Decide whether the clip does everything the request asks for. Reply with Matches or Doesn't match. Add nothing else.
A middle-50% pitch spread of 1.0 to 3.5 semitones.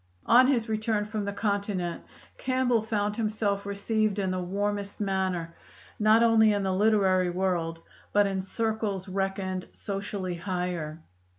Matches